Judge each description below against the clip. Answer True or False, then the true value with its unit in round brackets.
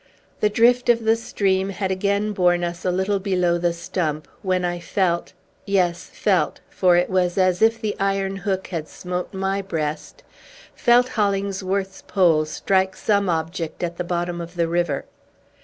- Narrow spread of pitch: True (2.3 semitones)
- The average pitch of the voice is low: False (185 Hz)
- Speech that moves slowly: False (165 wpm)